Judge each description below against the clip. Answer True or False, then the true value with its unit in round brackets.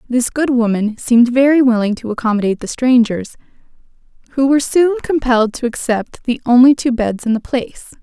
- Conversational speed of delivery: True (170 wpm)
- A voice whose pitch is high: True (245 Hz)